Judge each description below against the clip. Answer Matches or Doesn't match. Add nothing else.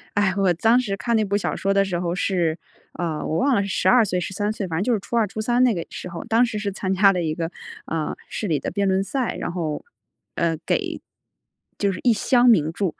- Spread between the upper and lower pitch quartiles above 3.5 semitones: Matches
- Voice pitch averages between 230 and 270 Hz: Doesn't match